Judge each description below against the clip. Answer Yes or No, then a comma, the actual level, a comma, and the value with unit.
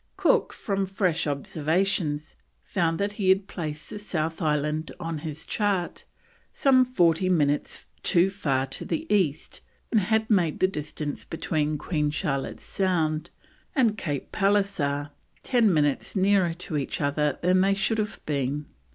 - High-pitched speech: No, medium, 170 Hz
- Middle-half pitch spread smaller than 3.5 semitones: No, average, 4.7 semitones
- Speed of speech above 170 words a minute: No, average, 145 wpm